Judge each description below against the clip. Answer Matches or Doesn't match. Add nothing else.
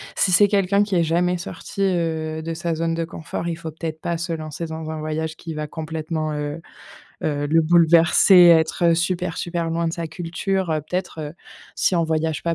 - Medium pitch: Matches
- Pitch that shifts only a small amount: Matches